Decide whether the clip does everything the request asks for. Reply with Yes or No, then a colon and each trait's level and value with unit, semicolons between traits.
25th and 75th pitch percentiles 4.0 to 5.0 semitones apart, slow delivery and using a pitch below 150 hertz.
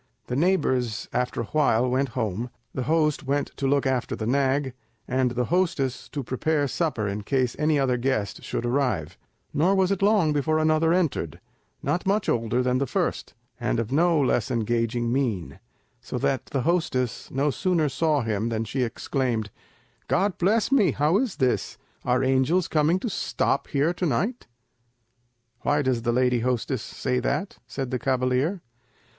No: average, 4.3 semitones; average, 170 wpm; low, 135 Hz